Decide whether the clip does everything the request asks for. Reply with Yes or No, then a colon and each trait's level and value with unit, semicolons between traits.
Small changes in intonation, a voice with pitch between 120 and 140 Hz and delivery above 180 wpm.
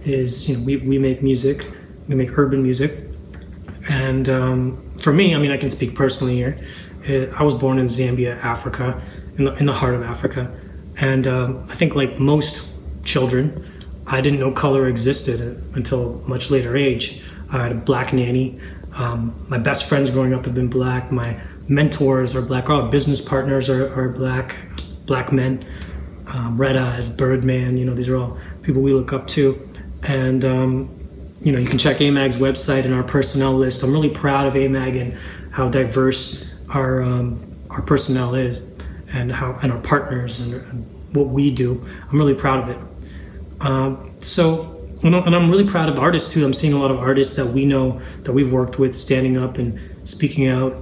Yes: narrow, 1.7 semitones; low, 130 Hz; average, 190 wpm